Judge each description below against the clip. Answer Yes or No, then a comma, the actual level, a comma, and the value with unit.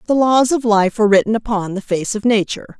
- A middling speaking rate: No, fast, 235 wpm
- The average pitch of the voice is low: No, high, 215 Hz